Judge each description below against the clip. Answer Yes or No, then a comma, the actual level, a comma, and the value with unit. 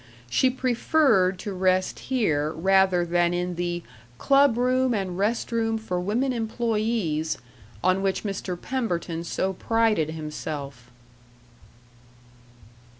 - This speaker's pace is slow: Yes, slow, 110 wpm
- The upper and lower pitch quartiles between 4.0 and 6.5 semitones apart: Yes, average, 4.8 semitones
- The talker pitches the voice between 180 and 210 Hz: Yes, high, 190 Hz